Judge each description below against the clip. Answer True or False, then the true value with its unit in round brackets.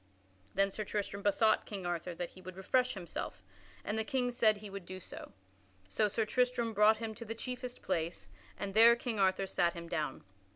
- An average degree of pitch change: True (3.6 semitones)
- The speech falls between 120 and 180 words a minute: False (200 wpm)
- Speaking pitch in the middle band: False (205 Hz)